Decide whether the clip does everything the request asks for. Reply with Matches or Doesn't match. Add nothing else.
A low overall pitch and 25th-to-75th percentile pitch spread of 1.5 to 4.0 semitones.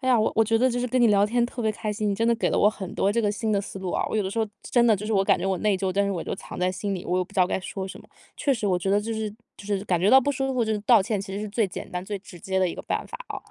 Doesn't match